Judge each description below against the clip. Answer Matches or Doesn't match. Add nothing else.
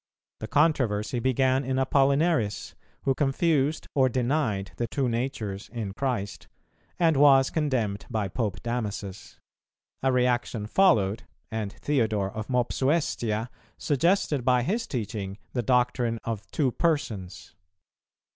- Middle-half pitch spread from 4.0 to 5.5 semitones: Matches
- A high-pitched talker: Doesn't match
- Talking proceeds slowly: Matches